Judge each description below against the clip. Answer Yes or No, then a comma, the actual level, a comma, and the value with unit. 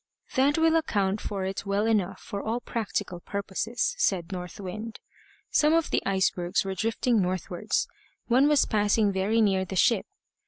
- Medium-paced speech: Yes, average, 160 wpm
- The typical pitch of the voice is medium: No, high, 205 Hz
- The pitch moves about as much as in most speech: Yes, average, 3.4 semitones